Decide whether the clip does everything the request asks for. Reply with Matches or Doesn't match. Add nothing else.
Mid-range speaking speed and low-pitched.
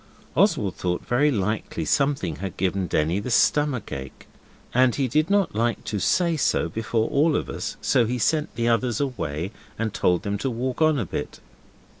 Matches